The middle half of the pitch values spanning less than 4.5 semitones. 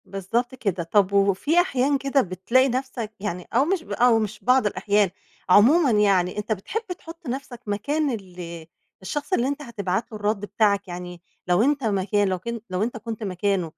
No: average, 5.1 semitones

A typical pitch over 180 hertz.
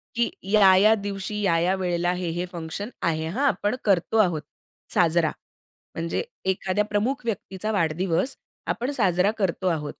Yes: high, 190 Hz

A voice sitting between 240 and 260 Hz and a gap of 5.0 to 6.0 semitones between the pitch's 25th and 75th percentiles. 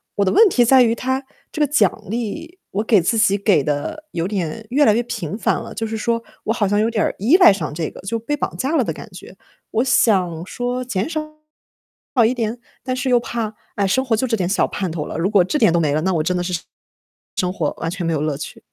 No: high, 215 Hz; average, 5.3 semitones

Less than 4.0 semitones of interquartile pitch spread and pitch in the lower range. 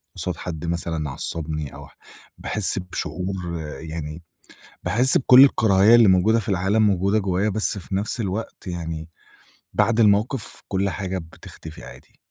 No: average, 4.4 semitones; very low, 95 Hz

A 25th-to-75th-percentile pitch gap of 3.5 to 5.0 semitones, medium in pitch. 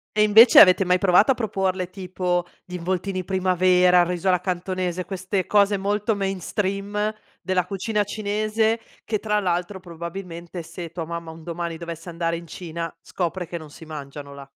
No: narrow, 2.6 semitones; medium, 180 Hz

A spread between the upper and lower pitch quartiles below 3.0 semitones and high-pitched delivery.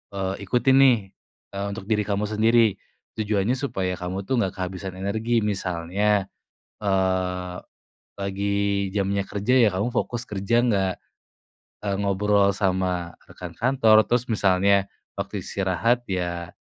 No: narrow, 2.5 semitones; low, 100 Hz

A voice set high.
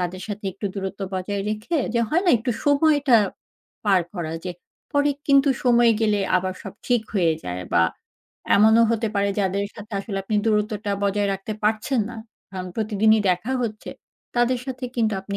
Yes: high, 215 Hz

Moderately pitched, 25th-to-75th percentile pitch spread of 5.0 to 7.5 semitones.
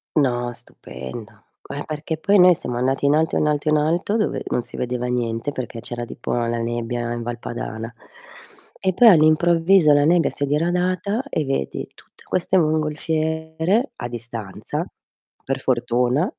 Yes: medium, 145 Hz; average, 5.3 semitones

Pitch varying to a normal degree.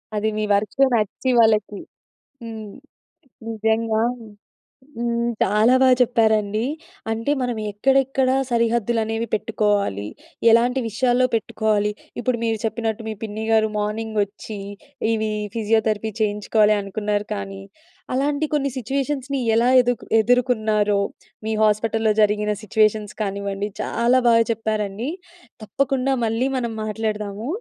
No: narrow, 2.1 semitones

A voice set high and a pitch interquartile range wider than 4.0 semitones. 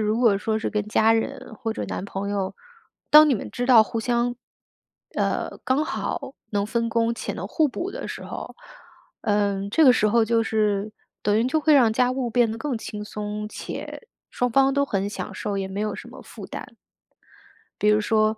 No: high, 225 Hz; average, 2.9 semitones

